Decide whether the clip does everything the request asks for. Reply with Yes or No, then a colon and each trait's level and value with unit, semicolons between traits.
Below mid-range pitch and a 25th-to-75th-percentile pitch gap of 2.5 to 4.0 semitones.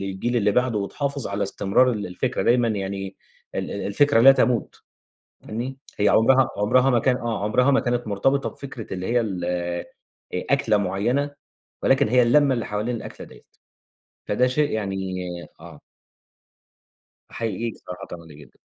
No: low, 115 Hz; average, 4.6 semitones